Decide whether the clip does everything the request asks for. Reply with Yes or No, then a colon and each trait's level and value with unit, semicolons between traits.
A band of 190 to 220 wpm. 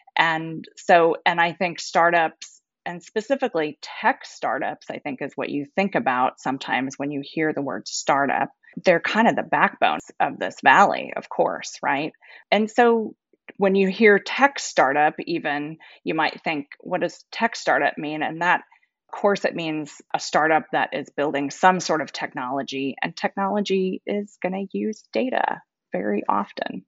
No: average, 165 wpm